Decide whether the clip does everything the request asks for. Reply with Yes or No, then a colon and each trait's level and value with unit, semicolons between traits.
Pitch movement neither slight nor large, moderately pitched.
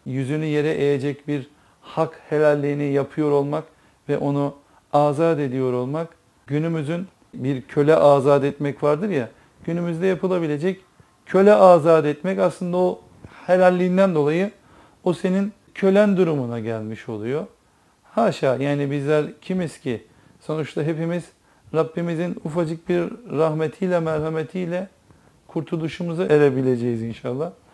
Yes: average, 3.8 semitones; medium, 155 Hz